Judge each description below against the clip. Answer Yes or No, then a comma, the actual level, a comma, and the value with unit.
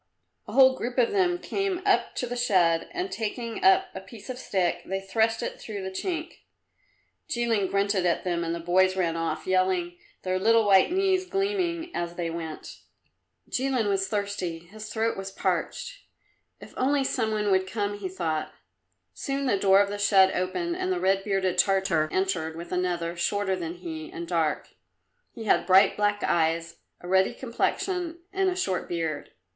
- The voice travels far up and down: Yes, wide, 5.7 semitones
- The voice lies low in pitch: No, high, 195 Hz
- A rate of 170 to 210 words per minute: Yes, average, 180 wpm